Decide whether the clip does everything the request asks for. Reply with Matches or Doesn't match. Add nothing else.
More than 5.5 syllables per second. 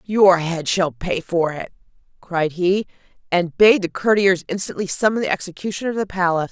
Doesn't match